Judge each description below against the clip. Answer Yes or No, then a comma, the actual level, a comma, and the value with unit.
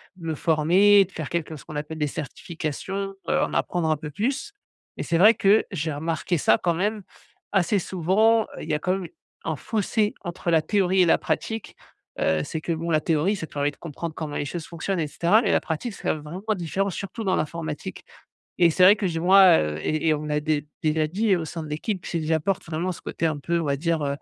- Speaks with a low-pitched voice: No, medium, 170 Hz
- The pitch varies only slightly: No, average, 3.7 semitones